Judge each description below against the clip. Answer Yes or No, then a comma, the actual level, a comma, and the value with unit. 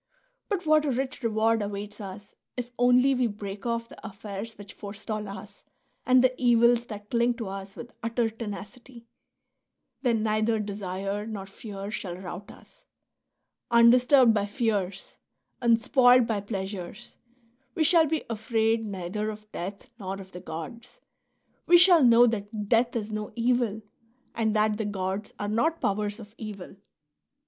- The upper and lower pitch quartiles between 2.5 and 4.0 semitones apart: Yes, average, 2.9 semitones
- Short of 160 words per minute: Yes, average, 150 wpm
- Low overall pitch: No, high, 220 Hz